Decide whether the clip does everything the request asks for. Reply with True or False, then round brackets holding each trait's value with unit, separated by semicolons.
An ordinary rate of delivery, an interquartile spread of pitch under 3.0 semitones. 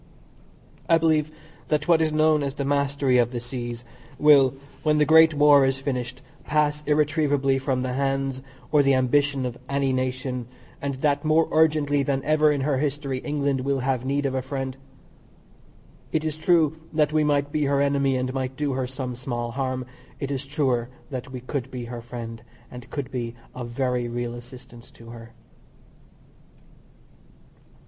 True (170 wpm; 2.6 semitones)